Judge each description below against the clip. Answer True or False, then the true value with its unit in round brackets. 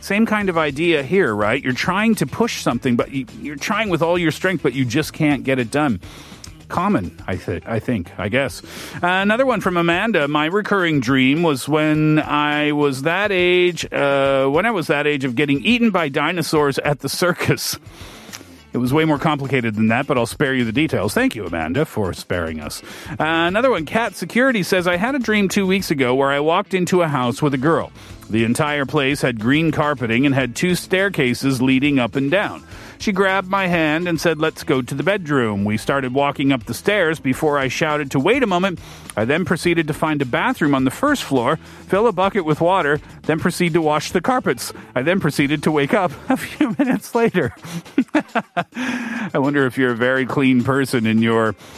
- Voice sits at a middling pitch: True (150 Hz)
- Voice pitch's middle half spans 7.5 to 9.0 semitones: False (5.3 semitones)